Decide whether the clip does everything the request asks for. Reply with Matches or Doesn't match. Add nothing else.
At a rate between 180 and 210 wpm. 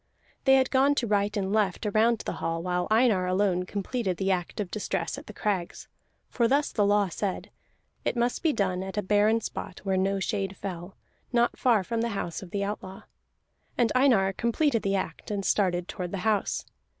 Matches